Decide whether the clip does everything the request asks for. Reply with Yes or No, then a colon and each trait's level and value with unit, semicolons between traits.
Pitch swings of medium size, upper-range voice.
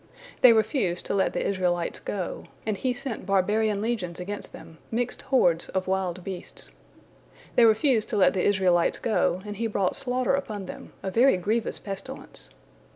Yes: average, 3.7 semitones; high, 205 Hz